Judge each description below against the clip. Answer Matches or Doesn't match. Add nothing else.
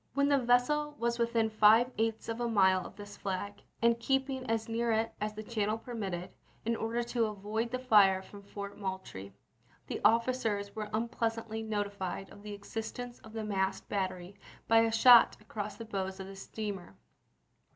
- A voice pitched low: Doesn't match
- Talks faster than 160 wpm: Matches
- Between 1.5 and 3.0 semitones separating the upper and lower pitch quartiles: Matches